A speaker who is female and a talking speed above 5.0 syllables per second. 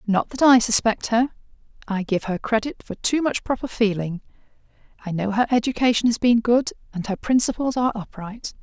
Yes: female; 5.5 syllables/s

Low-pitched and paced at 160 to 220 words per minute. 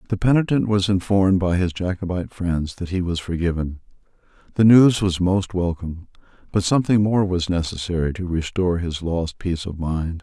Yes: very low, 90 Hz; average, 170 wpm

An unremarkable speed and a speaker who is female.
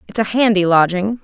Yes: average, 195 wpm; female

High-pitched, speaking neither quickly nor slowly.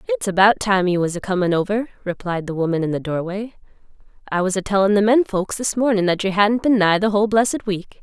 No: high, 195 Hz; fast, 230 wpm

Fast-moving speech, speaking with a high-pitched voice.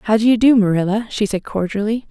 Yes: fast, 230 wpm; high, 210 Hz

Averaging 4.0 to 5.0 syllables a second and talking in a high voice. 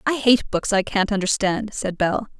Yes: 4.6 syllables/s; high, 205 Hz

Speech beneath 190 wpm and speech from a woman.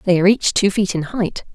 No: fast, 275 wpm; female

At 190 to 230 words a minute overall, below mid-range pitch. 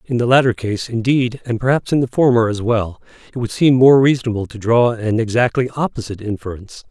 Yes: average, 200 wpm; low, 120 Hz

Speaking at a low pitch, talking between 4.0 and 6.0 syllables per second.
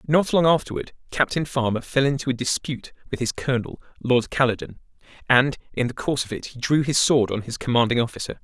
No: low, 130 Hz; 6.2 syllables/s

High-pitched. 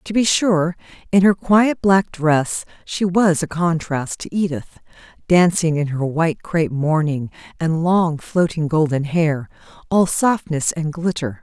No: medium, 165 Hz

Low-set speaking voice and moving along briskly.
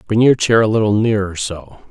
No: low, 105 Hz; average, 190 wpm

